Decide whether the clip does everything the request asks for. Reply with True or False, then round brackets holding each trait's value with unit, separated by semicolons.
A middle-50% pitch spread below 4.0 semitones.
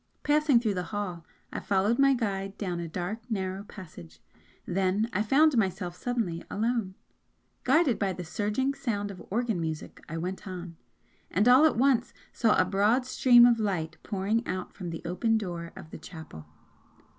False (4.7 semitones)